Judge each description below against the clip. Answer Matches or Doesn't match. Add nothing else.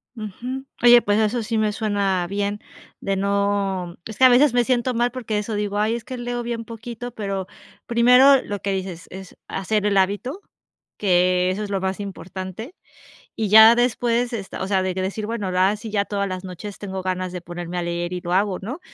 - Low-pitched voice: Doesn't match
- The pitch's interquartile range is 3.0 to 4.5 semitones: Matches